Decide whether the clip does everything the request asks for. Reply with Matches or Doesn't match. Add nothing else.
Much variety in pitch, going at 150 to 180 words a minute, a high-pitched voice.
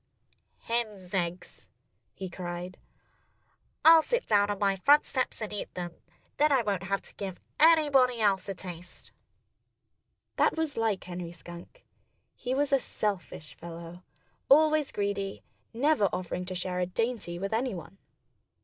Doesn't match